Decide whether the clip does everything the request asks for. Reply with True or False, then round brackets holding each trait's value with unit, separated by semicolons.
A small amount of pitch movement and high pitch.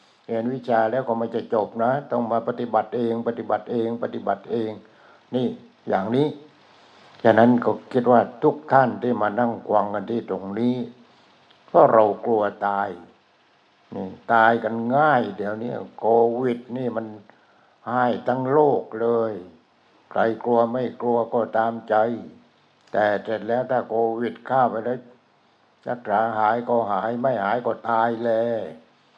False (1.4 semitones; 115 Hz)